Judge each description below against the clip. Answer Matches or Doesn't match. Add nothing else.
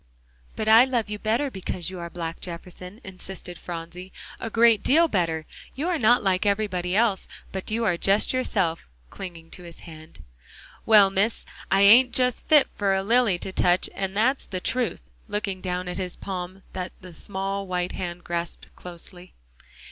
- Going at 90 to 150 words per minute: Doesn't match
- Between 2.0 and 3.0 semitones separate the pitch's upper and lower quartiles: Doesn't match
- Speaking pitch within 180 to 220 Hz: Matches